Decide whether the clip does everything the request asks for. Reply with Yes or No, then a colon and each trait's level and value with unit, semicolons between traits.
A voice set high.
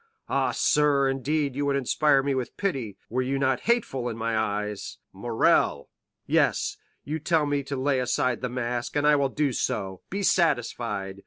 No: low, 135 Hz